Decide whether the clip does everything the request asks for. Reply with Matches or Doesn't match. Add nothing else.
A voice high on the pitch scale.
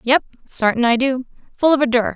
Matches